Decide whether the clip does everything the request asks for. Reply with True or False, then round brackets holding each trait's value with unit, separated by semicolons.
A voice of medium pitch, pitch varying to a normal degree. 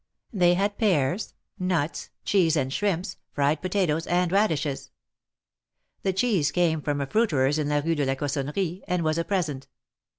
True (165 Hz; 4.2 semitones)